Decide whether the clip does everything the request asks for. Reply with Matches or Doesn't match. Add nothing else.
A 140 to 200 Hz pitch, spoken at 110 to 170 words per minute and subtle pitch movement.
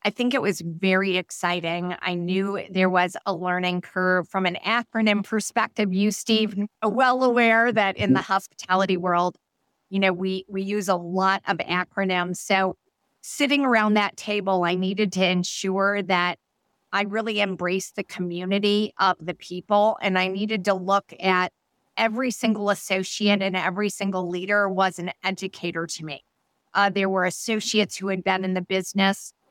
Matches